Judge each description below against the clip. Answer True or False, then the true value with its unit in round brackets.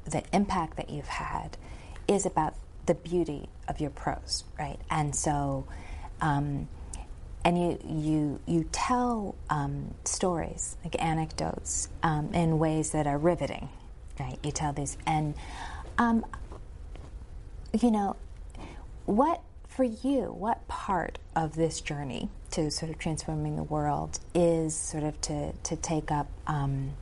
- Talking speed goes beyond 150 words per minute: False (135 wpm)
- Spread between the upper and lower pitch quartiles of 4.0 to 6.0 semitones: False (2.6 semitones)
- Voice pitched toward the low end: False (155 Hz)